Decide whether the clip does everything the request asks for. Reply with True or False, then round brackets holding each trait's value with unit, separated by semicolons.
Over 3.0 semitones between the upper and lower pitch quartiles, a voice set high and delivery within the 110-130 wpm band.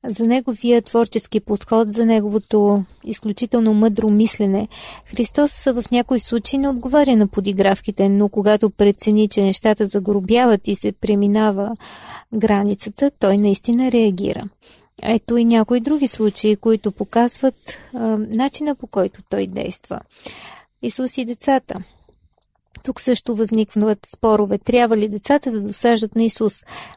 False (2.6 semitones; 220 Hz; 125 wpm)